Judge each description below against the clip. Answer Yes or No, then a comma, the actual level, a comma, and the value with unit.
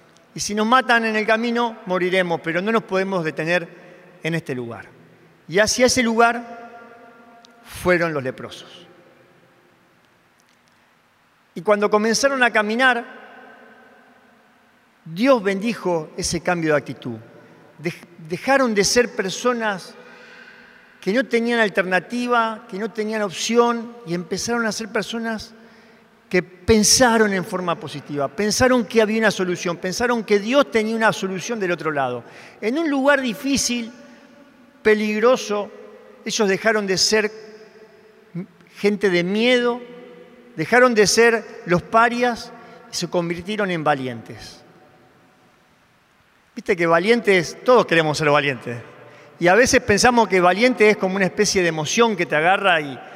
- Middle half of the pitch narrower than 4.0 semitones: No, average, 4.9 semitones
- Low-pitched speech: No, high, 215 Hz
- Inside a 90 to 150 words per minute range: Yes, average, 130 wpm